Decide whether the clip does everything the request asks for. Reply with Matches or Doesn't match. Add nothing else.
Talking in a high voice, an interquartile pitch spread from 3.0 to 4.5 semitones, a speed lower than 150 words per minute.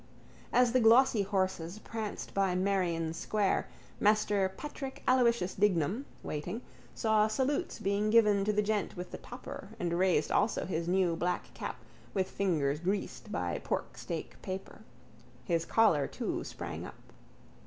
Matches